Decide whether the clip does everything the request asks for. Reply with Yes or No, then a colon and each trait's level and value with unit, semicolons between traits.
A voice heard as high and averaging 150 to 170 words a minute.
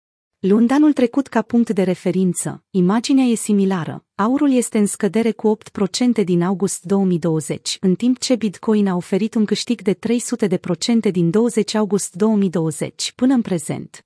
Yes: high, 205 Hz; average, 155 wpm